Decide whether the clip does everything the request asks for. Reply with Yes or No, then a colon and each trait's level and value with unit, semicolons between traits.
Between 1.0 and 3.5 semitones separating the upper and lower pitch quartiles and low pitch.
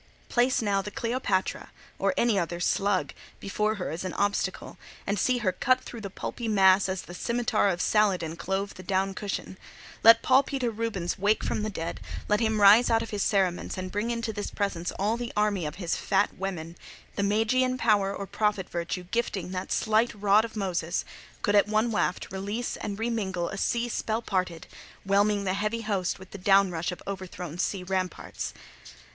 No: average, 2.9 semitones; high, 200 Hz